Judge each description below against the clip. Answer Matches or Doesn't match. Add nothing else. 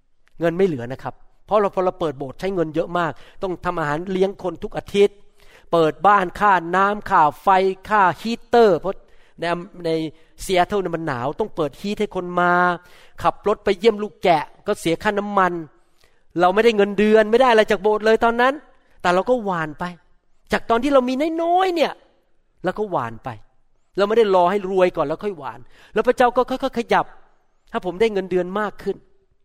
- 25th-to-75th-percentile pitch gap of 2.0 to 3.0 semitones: Doesn't match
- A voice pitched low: Doesn't match